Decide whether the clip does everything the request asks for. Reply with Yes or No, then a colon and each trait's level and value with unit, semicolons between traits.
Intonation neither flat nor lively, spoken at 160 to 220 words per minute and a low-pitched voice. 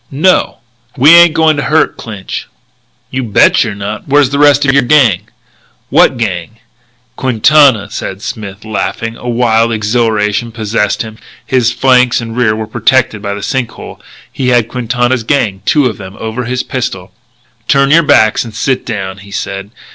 Yes: average, 3.9 semitones; average, 170 wpm; low, 115 Hz